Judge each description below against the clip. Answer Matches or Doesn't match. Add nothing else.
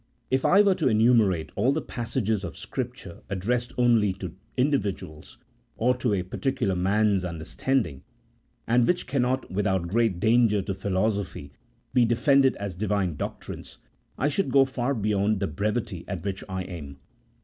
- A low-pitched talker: Matches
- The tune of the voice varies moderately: Matches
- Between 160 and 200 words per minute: Doesn't match